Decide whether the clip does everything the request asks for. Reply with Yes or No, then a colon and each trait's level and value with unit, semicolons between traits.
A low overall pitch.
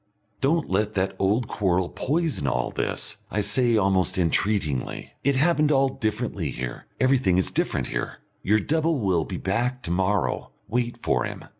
Yes: low, 105 Hz